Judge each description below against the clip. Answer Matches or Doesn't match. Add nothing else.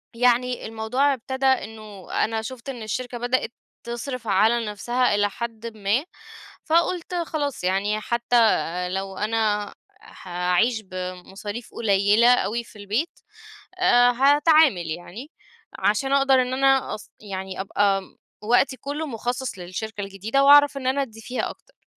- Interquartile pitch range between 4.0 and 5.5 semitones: Matches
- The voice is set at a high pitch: Matches